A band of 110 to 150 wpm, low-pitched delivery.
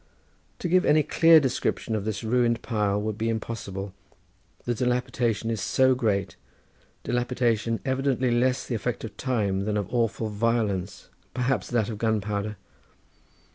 Yes: average, 140 wpm; low, 115 Hz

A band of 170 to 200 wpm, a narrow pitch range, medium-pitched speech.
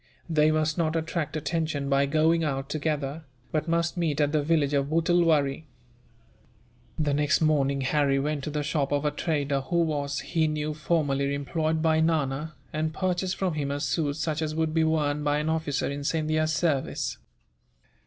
Yes: average, 175 wpm; narrow, 1.9 semitones; medium, 155 Hz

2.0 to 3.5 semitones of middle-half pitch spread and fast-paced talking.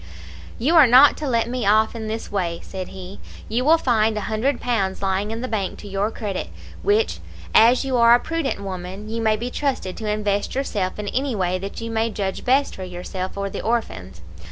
No: average, 3.9 semitones; fast, 215 wpm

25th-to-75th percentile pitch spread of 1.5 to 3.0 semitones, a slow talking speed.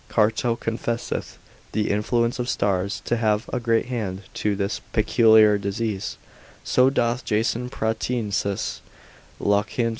Yes: narrow, 2.5 semitones; slow, 125 wpm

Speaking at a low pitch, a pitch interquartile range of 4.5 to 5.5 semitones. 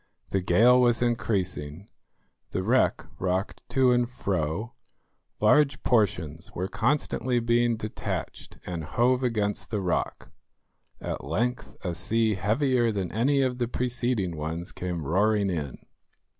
Yes: low, 110 Hz; average, 5.2 semitones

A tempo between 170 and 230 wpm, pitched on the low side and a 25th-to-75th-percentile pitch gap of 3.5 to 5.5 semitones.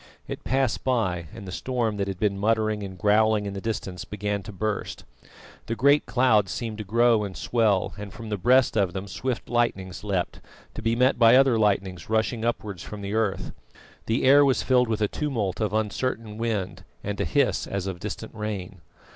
No: average, 195 wpm; low, 110 Hz; average, 3.0 semitones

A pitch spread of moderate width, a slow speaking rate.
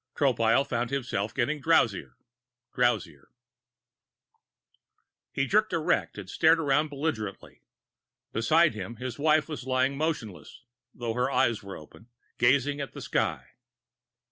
Yes: average, 4.8 semitones; slow, 120 wpm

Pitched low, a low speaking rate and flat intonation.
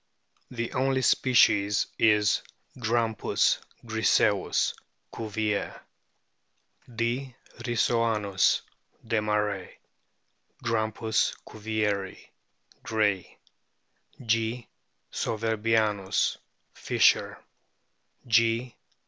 Yes: low, 110 Hz; slow, 55 wpm; narrow, 1.7 semitones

